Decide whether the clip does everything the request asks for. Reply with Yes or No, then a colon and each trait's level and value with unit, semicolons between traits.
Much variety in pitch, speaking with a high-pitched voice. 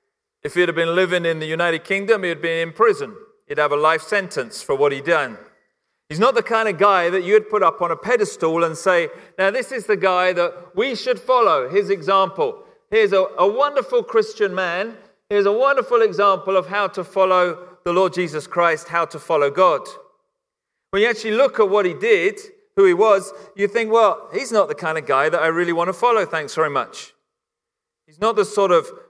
Yes: wide, 8.0 semitones; high, 200 Hz